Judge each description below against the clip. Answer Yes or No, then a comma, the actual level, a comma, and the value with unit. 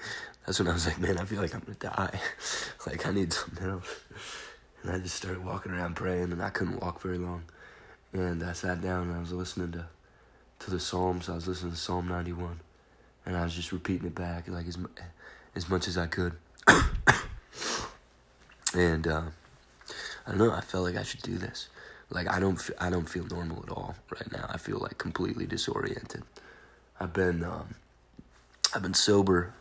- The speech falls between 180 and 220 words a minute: Yes, average, 195 wpm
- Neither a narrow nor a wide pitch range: No, narrow, 1.2 semitones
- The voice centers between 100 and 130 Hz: No, very low, 90 Hz